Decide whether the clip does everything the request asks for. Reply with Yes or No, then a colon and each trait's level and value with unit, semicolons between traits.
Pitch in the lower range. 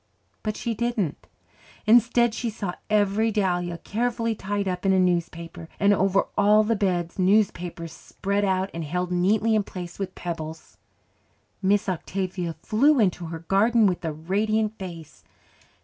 No: high, 195 Hz